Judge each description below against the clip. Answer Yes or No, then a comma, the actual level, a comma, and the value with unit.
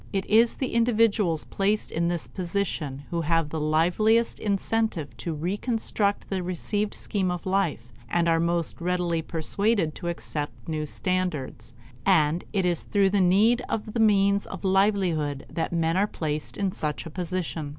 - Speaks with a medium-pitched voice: Yes, medium, 180 Hz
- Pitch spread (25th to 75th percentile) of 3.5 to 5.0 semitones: Yes, average, 3.8 semitones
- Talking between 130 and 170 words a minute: Yes, average, 160 wpm